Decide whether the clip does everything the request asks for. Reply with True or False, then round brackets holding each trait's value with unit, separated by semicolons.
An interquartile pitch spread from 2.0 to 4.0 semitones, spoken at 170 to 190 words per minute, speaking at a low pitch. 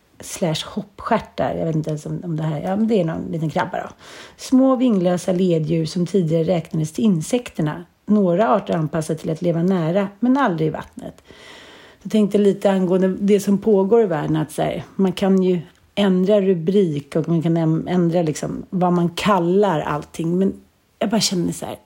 False (3.7 semitones; 185 wpm; 180 Hz)